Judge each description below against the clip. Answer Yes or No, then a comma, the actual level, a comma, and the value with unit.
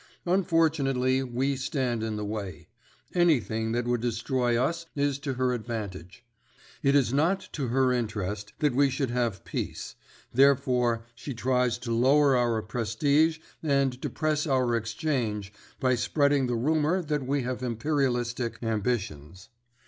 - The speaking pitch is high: No, low, 125 Hz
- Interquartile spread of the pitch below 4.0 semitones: Yes, average, 3.5 semitones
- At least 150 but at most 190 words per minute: No, average, 140 wpm